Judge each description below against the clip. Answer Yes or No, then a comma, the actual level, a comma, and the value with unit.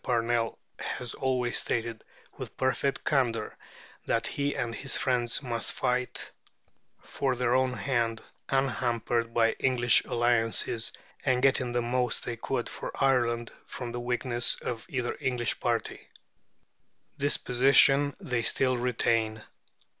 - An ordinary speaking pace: No, slow, 125 wpm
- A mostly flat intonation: Yes, narrow, 1.8 semitones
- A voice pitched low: Yes, low, 120 Hz